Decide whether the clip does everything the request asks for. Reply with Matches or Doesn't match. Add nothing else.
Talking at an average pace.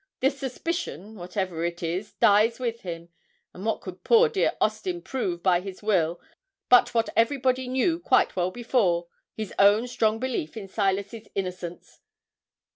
Matches